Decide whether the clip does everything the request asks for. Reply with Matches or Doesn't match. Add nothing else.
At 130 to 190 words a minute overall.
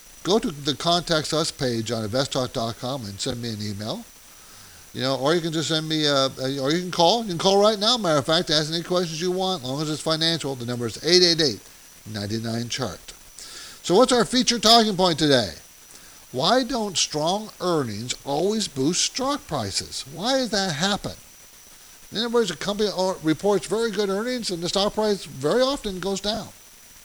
Doesn't match